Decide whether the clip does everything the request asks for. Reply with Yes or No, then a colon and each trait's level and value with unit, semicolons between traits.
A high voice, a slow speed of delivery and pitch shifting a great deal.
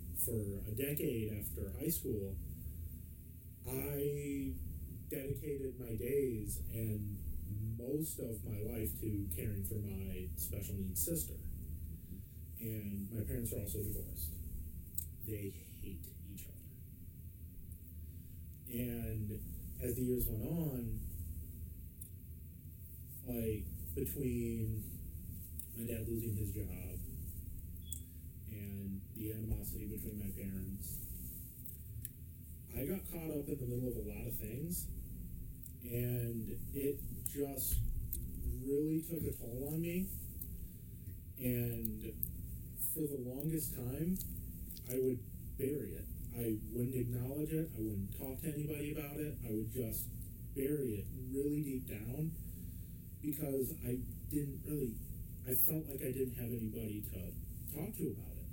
No: low, 105 Hz; slow, 115 wpm; wide, 6.2 semitones